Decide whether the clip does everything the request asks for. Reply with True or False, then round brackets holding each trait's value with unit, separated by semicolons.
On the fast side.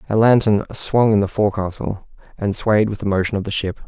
True (215 wpm)